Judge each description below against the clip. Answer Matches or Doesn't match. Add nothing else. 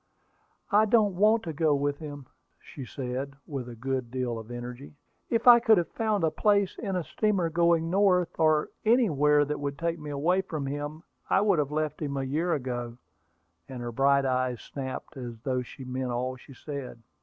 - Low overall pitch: Doesn't match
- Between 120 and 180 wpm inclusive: Doesn't match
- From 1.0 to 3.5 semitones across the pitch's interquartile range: Doesn't match